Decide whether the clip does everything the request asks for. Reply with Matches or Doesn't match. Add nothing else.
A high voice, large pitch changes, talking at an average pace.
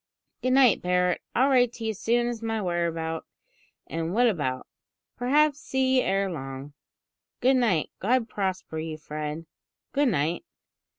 Matches